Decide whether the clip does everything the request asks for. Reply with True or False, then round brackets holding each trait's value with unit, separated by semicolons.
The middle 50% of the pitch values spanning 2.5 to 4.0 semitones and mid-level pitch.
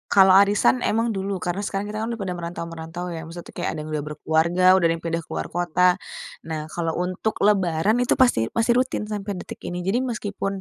True (3.5 semitones; 180 Hz)